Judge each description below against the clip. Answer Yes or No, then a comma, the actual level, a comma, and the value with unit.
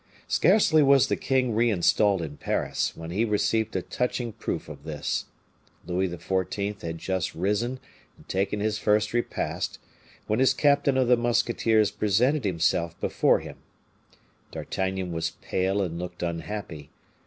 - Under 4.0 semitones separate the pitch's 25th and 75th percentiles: No, average, 5.1 semitones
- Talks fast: No, average, 145 wpm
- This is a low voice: Yes, low, 105 Hz